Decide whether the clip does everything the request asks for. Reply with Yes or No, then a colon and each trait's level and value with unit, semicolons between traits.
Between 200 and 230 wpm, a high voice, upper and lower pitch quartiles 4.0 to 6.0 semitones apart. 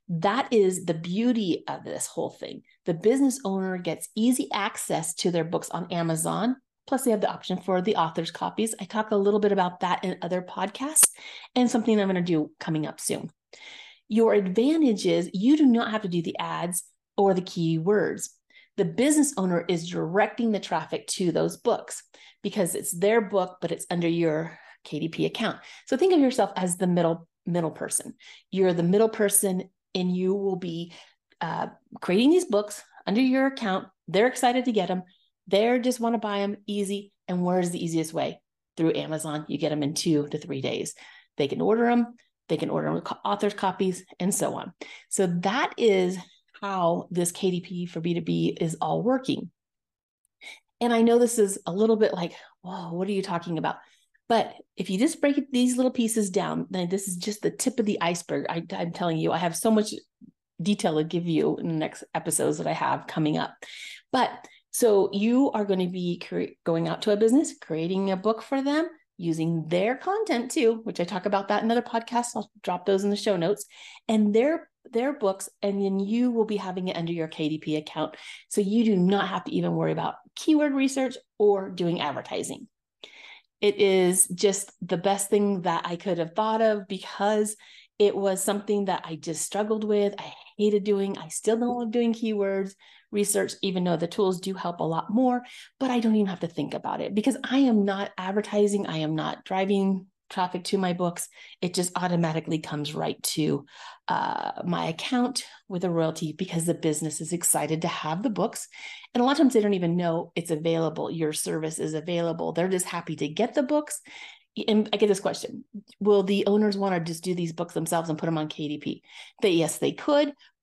Yes: fast, 205 wpm; high, 195 Hz; average, 4.5 semitones